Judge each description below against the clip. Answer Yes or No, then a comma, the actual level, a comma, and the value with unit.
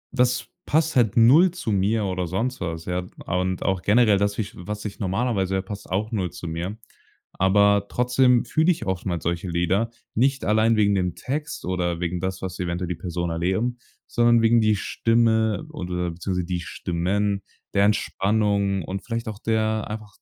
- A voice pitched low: Yes, low, 100 Hz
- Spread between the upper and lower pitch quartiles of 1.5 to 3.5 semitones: No, average, 3.9 semitones